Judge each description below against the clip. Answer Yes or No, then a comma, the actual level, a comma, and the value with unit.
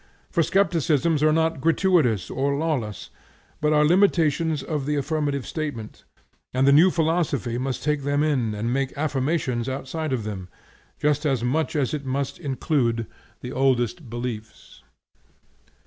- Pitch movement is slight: No, average, 3.7 semitones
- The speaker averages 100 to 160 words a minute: Yes, average, 145 wpm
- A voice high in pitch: No, medium, 140 Hz